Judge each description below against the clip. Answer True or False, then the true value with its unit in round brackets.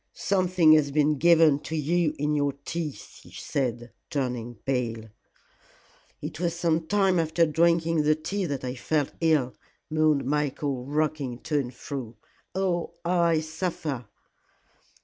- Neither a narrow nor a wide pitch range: True (3.3 semitones)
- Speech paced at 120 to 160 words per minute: True (140 wpm)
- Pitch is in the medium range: True (155 Hz)